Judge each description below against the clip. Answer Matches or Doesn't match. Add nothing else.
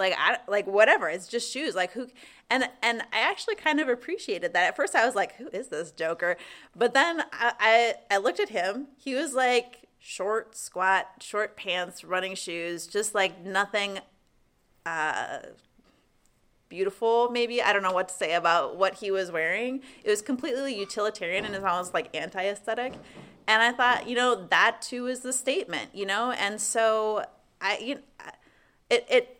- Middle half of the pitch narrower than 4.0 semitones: Doesn't match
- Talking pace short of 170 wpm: Doesn't match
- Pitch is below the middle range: Doesn't match